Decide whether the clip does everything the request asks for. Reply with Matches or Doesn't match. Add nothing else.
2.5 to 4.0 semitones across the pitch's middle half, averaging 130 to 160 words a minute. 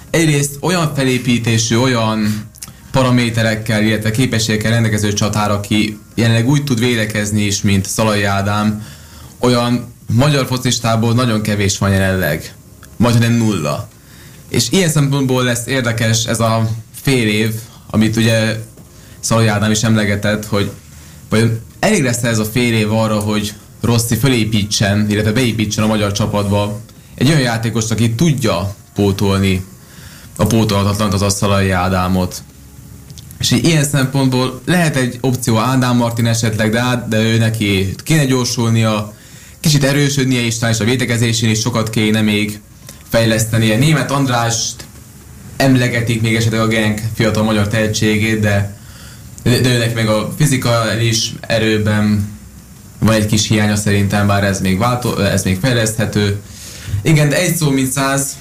Matches